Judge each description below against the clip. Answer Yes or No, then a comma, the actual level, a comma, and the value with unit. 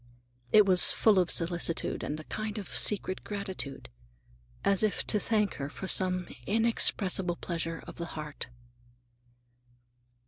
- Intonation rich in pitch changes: No, average, 3.8 semitones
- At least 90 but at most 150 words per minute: Yes, slow, 135 wpm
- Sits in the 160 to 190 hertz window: Yes, medium, 185 Hz